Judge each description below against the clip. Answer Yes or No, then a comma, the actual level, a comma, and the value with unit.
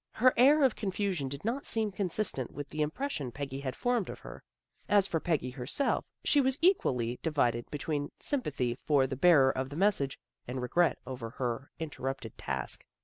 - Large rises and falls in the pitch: Yes, wide, 7.8 semitones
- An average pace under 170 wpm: No, average, 175 wpm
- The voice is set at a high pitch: No, medium, 150 Hz